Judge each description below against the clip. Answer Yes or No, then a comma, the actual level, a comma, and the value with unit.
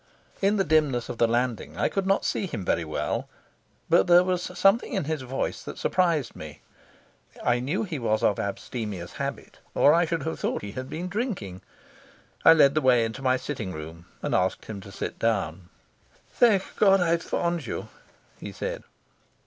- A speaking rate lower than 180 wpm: No, average, 185 wpm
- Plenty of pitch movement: Yes, wide, 8.2 semitones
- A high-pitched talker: No, low, 130 Hz